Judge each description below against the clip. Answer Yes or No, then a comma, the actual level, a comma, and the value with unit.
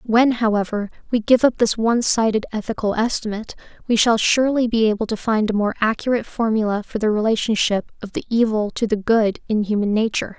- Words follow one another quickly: No, average, 190 wpm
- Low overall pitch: No, high, 220 Hz